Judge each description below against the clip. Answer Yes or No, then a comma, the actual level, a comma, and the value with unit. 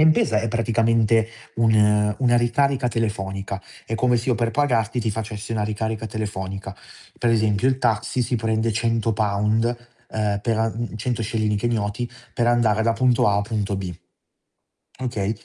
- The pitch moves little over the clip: Yes, narrow, 2.0 semitones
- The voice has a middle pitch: No, low, 110 Hz